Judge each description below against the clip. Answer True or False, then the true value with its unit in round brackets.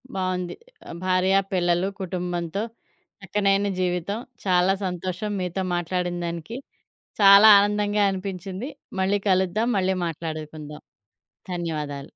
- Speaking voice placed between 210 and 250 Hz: False (185 Hz)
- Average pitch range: False (2.1 semitones)